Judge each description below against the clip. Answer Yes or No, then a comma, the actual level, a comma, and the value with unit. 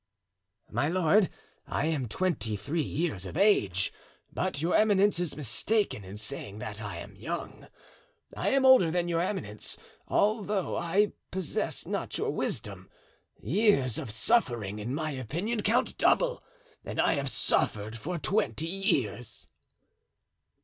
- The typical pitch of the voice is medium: Yes, medium, 160 Hz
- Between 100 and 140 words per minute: Yes, slow, 135 wpm